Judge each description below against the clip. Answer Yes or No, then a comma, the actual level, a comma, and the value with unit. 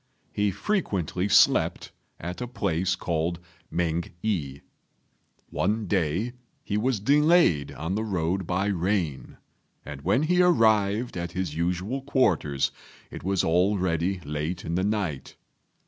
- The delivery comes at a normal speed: No, slow, 130 wpm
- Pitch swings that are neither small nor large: Yes, average, 4.2 semitones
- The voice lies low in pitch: Yes, very low, 95 Hz